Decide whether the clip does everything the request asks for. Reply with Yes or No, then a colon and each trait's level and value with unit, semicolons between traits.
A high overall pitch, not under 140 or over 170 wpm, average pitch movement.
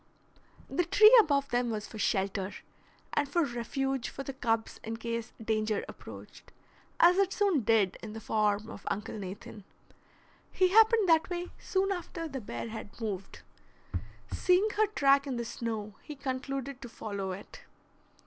No: high, 245 Hz; average, 160 wpm; wide, 7.3 semitones